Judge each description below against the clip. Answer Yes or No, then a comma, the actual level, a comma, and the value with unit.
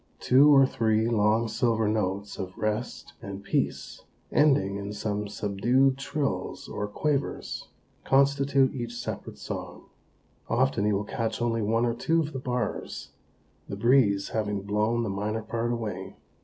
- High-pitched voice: No, low, 110 Hz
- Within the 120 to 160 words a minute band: Yes, average, 145 wpm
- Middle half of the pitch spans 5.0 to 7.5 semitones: No, average, 3.7 semitones